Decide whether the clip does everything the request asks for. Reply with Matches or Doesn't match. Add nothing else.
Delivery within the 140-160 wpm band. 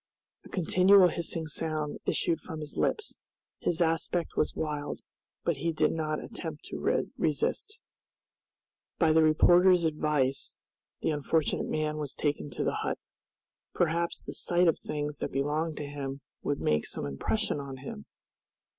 Matches